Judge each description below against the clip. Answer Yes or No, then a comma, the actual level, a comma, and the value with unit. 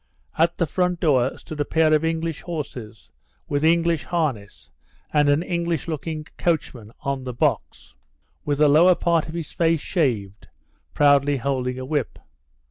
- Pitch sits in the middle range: Yes, medium, 150 Hz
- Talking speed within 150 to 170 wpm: Yes, average, 155 wpm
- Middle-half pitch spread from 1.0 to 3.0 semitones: No, average, 4.0 semitones